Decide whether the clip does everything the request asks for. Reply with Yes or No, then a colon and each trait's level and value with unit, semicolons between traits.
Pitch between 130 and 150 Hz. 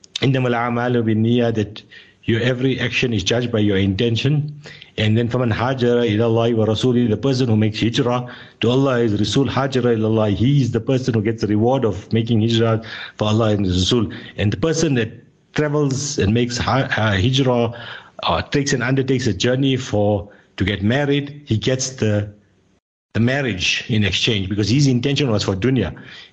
No: low, 120 Hz